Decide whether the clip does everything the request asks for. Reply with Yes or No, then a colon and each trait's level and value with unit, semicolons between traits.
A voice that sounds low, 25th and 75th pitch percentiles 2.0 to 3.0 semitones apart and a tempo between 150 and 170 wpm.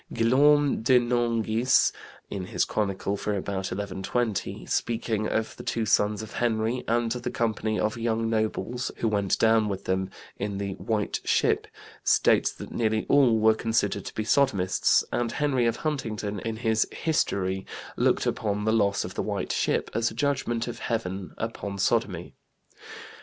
Yes: low, 110 Hz; narrow, 2.6 semitones; average, 160 wpm